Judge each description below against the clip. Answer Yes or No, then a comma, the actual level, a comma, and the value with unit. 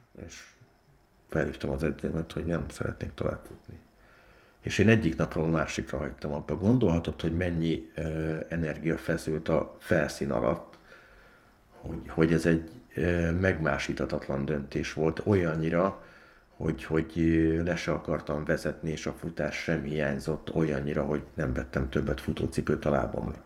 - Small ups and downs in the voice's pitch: Yes, narrow, 1.7 semitones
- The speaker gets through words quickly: No, average, 135 wpm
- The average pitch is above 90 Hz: No, very low, 80 Hz